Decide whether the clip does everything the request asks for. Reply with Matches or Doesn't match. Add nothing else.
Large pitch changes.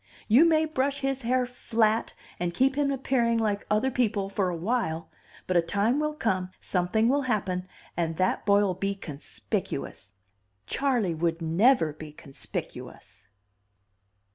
Matches